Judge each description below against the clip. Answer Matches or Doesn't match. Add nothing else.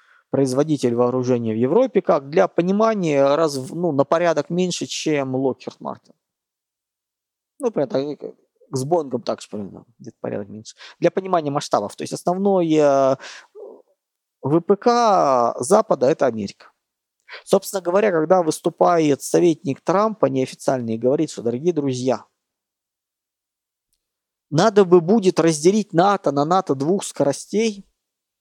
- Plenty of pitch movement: Matches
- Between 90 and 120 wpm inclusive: Matches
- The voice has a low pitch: Doesn't match